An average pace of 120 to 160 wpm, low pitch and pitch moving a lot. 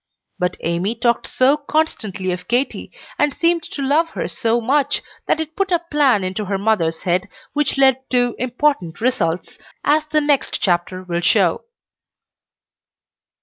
No: average, 150 wpm; high, 245 Hz; wide, 8.0 semitones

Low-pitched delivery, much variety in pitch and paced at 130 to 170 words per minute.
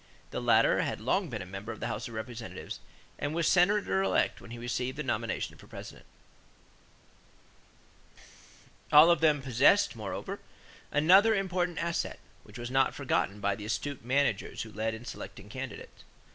Yes: low, 130 Hz; wide, 6.9 semitones; average, 160 wpm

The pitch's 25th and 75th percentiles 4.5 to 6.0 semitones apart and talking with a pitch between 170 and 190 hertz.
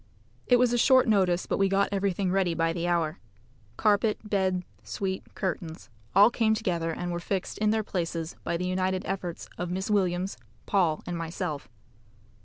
No: narrow, 2.6 semitones; medium, 185 Hz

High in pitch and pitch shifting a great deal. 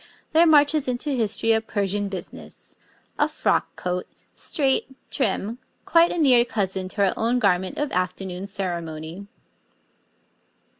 Yes: high, 205 Hz; wide, 5.9 semitones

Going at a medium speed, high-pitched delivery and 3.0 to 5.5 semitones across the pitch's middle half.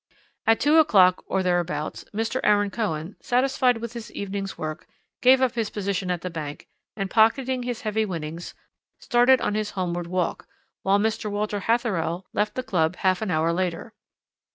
Yes: average, 170 wpm; high, 205 Hz; average, 4.1 semitones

